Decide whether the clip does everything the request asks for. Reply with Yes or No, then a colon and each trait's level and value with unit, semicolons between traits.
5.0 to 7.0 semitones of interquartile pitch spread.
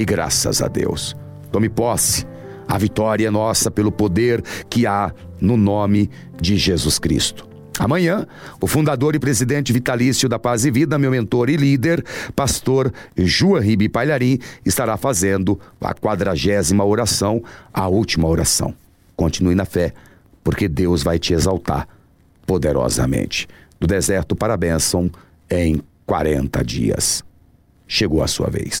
Yes: average, 5.3 semitones